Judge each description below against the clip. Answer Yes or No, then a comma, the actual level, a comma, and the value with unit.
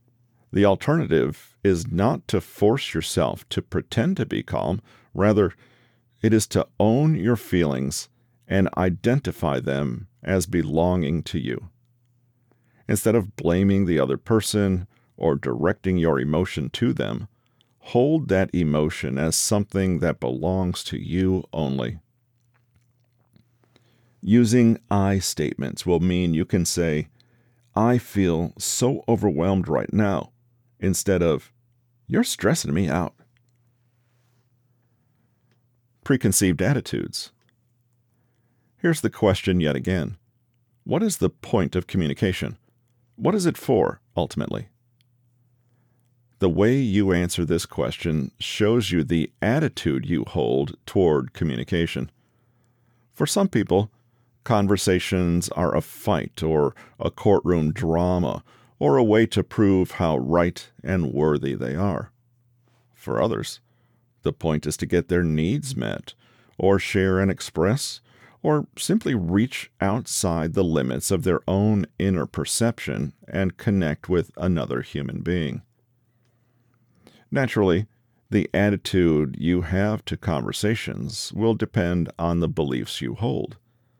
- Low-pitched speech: Yes, low, 105 Hz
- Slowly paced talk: Yes, slow, 120 wpm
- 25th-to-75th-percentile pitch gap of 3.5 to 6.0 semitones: Yes, average, 5.2 semitones